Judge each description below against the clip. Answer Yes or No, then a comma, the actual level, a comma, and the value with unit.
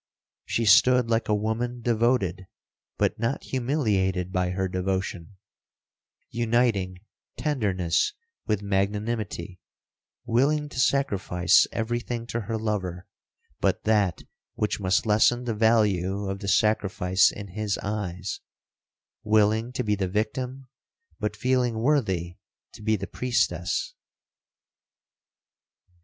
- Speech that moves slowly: Yes, slow, 105 wpm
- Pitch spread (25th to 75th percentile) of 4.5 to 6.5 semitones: No, average, 3.7 semitones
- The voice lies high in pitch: No, low, 105 Hz